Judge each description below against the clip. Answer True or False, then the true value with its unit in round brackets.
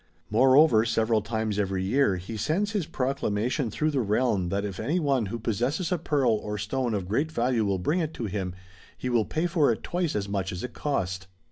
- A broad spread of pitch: True (5.8 semitones)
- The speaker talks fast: True (220 wpm)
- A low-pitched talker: True (115 Hz)